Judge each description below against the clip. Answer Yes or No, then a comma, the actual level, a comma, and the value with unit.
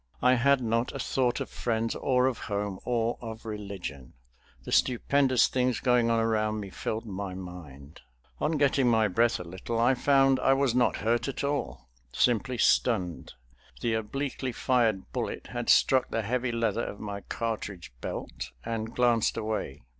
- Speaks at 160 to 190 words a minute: Yes, average, 165 wpm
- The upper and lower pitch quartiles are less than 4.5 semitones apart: Yes, average, 3.6 semitones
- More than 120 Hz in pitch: No, low, 115 Hz